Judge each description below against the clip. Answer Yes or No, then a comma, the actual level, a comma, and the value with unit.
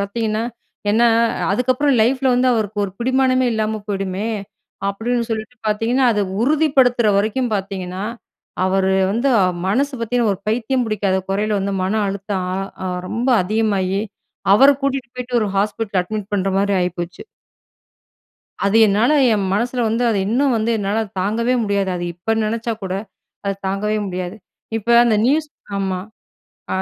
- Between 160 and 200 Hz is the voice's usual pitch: No, high, 215 Hz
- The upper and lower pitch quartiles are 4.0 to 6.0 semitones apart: No, average, 3.6 semitones